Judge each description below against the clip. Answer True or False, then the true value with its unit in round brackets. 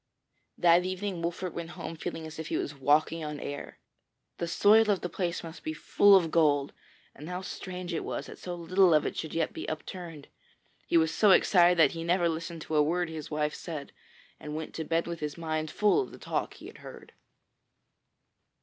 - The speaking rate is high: True (210 wpm)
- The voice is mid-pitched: True (165 Hz)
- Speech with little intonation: True (2.3 semitones)